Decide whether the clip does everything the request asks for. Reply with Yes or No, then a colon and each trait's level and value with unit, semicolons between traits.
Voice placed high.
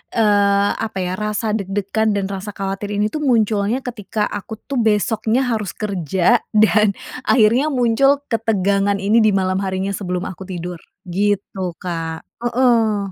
Yes: high, 205 Hz